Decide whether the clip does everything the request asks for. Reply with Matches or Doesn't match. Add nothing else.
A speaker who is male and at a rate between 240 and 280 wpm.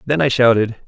Doesn't match